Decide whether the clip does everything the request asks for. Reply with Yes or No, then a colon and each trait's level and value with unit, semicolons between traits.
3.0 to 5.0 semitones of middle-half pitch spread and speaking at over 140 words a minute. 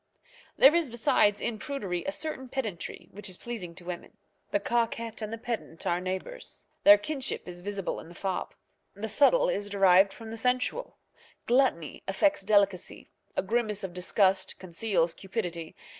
Yes: average, 4.5 semitones; average, 160 wpm